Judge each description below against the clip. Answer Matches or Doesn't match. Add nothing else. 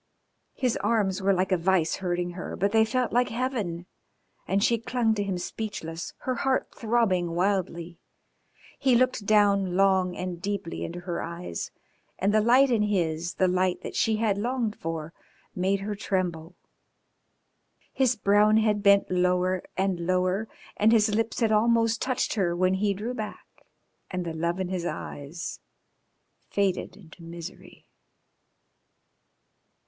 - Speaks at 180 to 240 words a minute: Doesn't match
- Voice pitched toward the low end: Doesn't match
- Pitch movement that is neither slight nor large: Matches